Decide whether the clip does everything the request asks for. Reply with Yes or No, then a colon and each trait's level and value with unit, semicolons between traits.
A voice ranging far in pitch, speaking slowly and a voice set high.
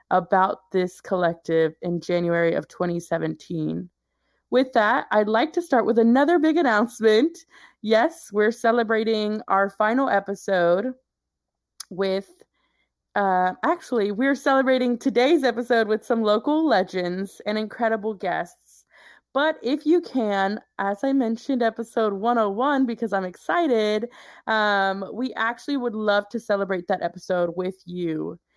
No: average, 5.0 semitones; slow, 125 wpm; high, 220 Hz